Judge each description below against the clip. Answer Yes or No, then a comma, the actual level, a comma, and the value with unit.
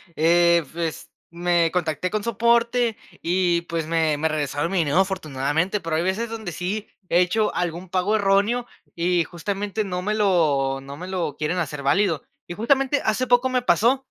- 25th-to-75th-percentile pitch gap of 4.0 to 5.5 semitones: Yes, average, 4.4 semitones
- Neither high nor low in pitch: Yes, medium, 180 Hz